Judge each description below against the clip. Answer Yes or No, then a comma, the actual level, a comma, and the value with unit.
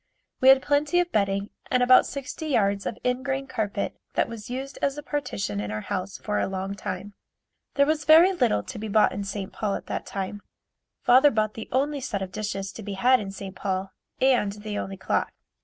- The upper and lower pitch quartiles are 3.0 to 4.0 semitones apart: No, average, 5.2 semitones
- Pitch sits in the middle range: No, high, 215 Hz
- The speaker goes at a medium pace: No, fast, 210 wpm